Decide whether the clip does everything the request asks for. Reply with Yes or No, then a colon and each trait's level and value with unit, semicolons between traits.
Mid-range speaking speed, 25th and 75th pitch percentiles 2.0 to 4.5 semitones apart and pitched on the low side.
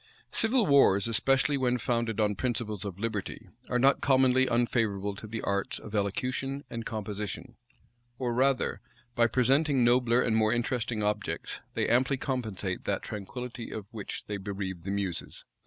Yes: average, 155 wpm; average, 3.7 semitones; low, 115 Hz